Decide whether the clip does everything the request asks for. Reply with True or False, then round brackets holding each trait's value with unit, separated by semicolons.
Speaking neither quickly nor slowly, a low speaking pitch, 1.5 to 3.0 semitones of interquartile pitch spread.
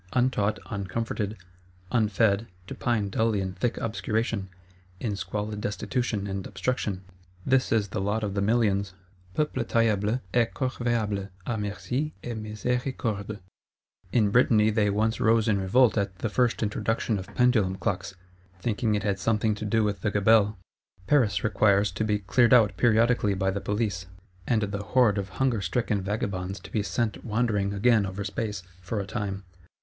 True (155 wpm; 105 Hz; 2.5 semitones)